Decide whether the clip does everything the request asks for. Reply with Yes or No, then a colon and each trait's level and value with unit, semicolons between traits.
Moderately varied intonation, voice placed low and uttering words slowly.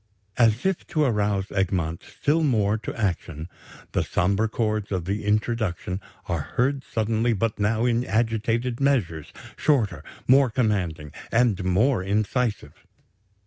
Yes: average, 3.9 semitones; low, 110 Hz; slow, 130 wpm